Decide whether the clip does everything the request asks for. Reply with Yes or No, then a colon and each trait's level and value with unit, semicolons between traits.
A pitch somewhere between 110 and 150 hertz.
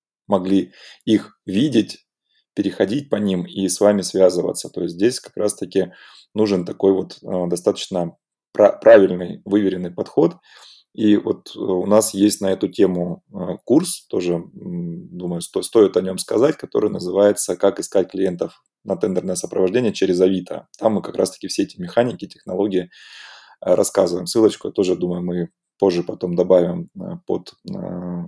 No: very low, 95 Hz